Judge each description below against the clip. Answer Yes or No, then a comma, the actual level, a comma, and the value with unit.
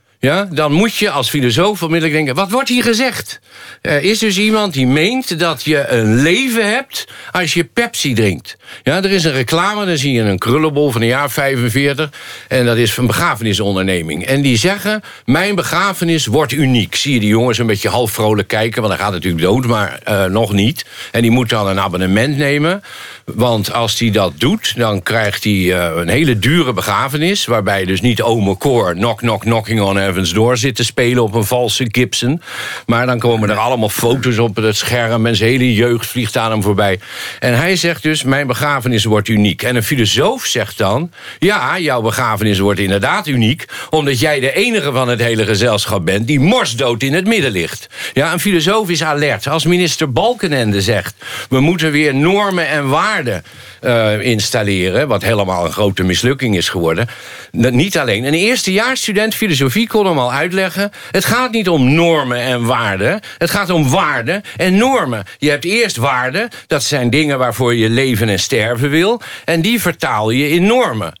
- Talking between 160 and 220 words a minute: Yes, average, 190 wpm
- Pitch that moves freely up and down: Yes, wide, 6.9 semitones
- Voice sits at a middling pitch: No, low, 125 Hz